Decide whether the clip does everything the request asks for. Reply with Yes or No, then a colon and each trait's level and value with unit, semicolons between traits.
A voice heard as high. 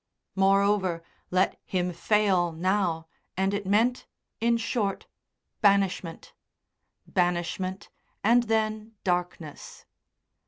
Yes: high, 195 Hz